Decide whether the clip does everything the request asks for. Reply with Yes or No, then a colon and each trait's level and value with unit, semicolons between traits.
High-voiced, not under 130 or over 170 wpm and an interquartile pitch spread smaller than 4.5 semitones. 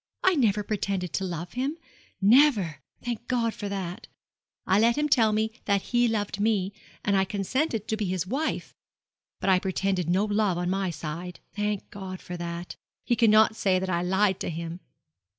No: high, 200 Hz; average, 185 wpm; average, 3.3 semitones